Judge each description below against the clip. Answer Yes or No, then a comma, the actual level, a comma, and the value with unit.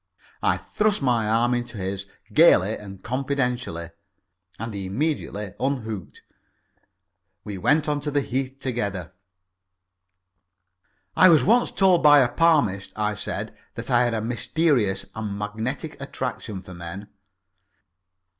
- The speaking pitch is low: Yes, low, 120 Hz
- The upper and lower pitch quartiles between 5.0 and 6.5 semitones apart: Yes, wide, 5.6 semitones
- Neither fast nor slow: No, slow, 125 wpm